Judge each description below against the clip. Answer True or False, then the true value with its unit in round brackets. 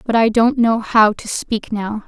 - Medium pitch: False (225 Hz)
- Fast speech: True (230 wpm)